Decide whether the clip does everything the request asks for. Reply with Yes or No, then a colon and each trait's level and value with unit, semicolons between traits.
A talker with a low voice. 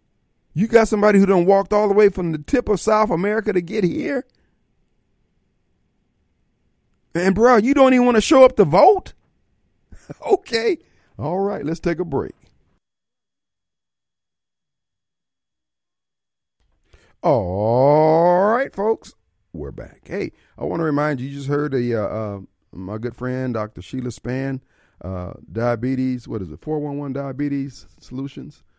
No: medium, 145 Hz